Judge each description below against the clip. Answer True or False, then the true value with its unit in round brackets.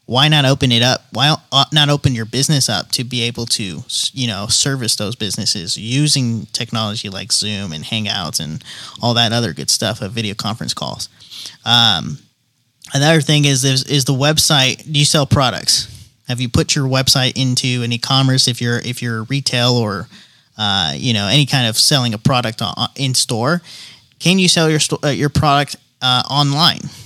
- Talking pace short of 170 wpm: False (180 wpm)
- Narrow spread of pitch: False (3.6 semitones)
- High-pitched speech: False (125 Hz)